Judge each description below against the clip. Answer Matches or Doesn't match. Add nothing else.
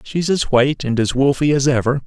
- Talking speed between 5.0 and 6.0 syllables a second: Matches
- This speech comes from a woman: Doesn't match